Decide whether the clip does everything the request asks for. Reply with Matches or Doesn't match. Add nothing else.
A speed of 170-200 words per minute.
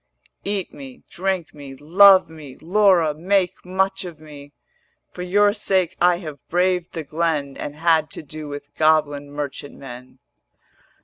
Doesn't match